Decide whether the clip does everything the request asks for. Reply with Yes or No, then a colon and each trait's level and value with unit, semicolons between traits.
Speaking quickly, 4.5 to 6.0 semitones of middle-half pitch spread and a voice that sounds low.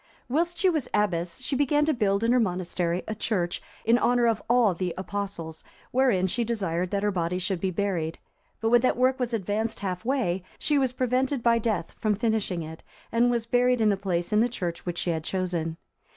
No: fast, 210 wpm; average, 5.2 semitones; high, 210 Hz